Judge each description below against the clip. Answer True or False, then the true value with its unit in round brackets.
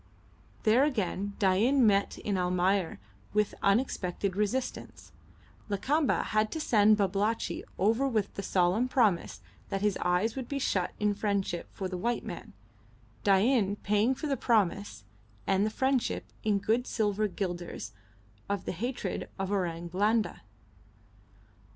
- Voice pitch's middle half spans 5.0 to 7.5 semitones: False (3.2 semitones)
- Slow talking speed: True (130 wpm)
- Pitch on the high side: True (205 Hz)